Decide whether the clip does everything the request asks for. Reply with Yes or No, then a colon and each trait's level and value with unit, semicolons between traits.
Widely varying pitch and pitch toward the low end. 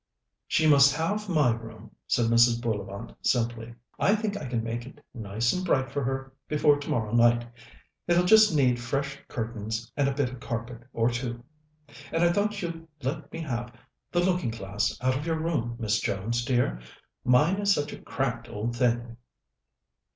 No: average, 4.8 semitones; low, 125 Hz